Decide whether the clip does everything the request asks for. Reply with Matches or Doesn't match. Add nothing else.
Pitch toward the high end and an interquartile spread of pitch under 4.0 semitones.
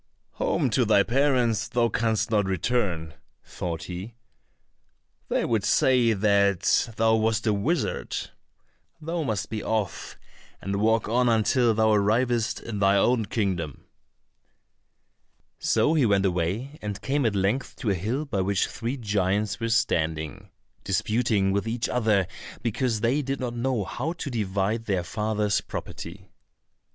Doesn't match